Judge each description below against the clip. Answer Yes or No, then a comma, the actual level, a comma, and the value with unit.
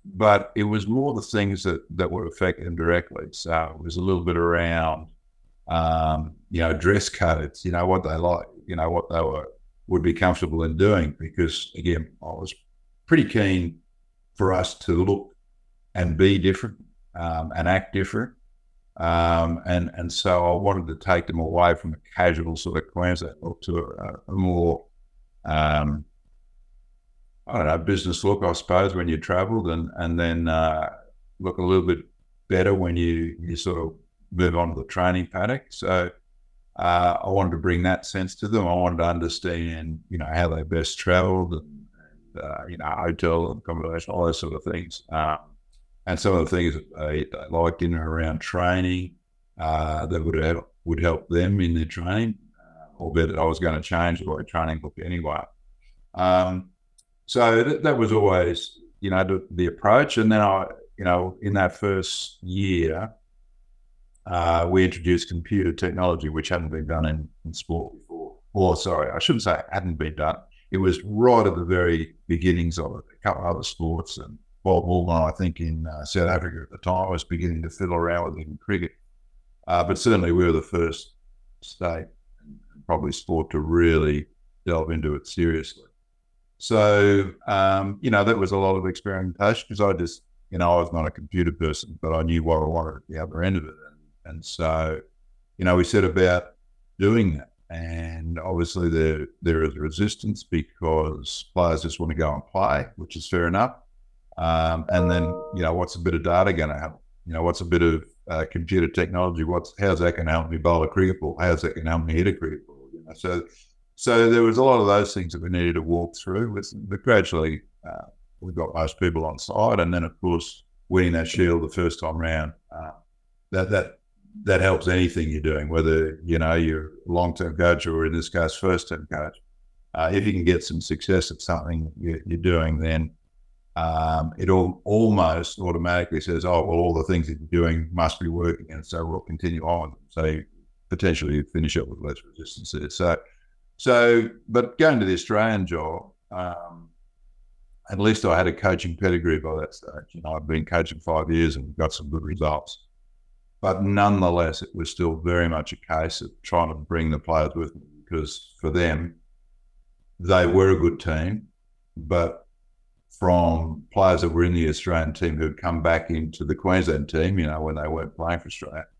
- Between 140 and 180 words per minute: No, average, 195 wpm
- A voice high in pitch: No, very low, 85 Hz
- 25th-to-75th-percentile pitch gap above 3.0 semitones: No, narrow, 2.5 semitones